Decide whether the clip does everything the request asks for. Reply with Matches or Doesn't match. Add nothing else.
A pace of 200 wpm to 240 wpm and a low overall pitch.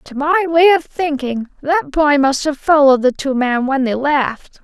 Doesn't match